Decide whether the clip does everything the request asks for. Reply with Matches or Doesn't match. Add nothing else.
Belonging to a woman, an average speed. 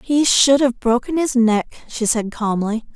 Matches